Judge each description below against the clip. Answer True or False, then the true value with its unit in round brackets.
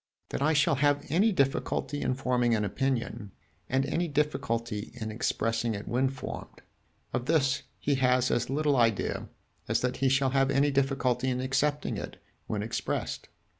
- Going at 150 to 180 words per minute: True (165 wpm)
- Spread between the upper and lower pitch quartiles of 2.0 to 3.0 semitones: True (2.7 semitones)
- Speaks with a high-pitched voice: False (130 Hz)